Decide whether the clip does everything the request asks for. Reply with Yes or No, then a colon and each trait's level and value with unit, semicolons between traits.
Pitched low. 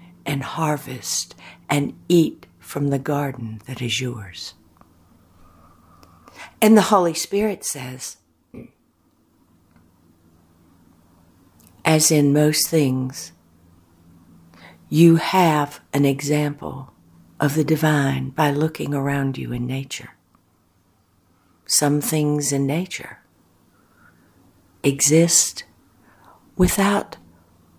Yes: low, 130 Hz